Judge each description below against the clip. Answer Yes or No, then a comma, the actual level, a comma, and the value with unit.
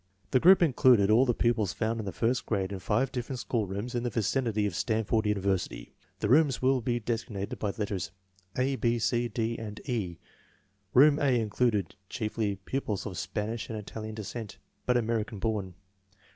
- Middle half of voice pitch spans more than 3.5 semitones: No, average, 3.0 semitones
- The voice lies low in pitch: Yes, low, 110 Hz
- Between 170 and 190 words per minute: Yes, average, 175 wpm